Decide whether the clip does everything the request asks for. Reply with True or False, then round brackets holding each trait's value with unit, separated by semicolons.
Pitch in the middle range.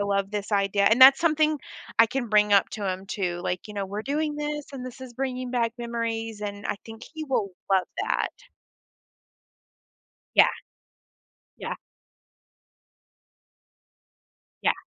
False (225 Hz)